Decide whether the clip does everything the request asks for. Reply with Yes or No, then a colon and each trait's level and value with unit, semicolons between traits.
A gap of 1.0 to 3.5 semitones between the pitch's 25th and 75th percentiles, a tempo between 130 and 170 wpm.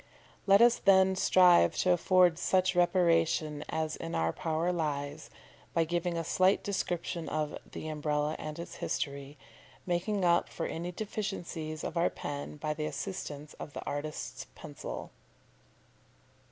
Yes: average, 3.0 semitones; average, 140 wpm